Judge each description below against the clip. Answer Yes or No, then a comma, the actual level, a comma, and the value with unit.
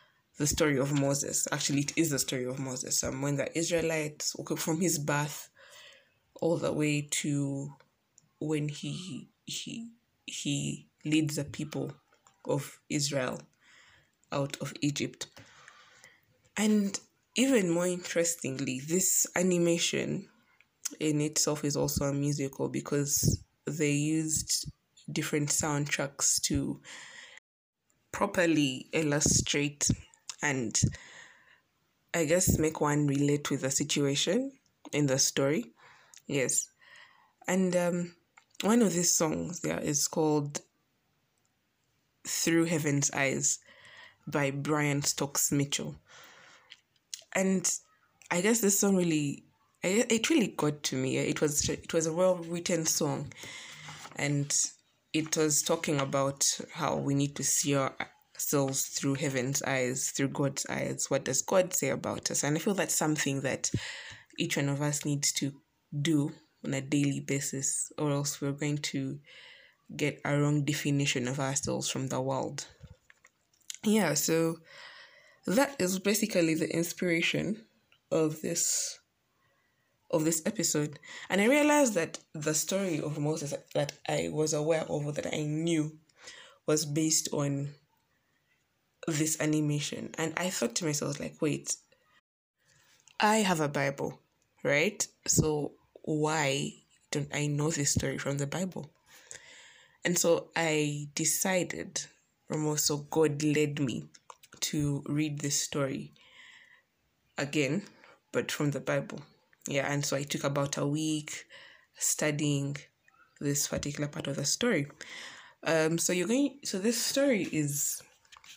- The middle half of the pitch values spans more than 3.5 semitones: No, average, 3.0 semitones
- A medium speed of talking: No, slow, 130 wpm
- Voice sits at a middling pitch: Yes, medium, 150 Hz